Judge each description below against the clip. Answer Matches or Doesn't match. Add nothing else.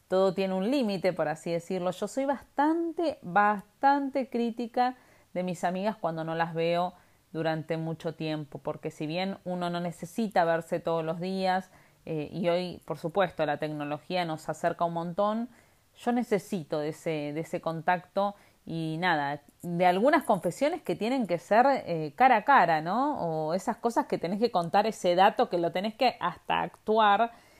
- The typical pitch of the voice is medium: Matches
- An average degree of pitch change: Matches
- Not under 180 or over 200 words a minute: Doesn't match